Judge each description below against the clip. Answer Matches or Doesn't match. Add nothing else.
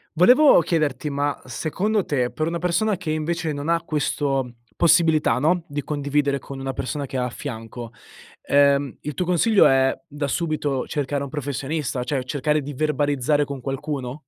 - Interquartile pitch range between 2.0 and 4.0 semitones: Matches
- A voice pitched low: Doesn't match